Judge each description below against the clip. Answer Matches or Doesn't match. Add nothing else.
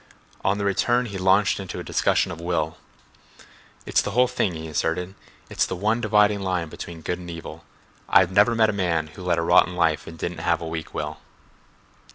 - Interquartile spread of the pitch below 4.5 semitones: Matches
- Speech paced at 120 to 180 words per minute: Doesn't match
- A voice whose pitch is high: Doesn't match